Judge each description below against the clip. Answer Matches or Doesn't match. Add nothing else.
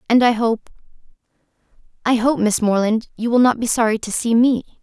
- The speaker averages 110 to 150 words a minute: Doesn't match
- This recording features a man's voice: Doesn't match